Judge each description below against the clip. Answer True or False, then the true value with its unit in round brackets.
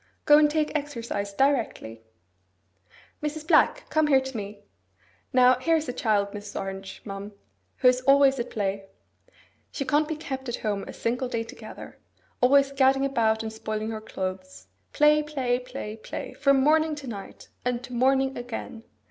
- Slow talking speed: False (165 wpm)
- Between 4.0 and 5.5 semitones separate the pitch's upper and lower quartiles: True (4.4 semitones)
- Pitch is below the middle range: False (250 Hz)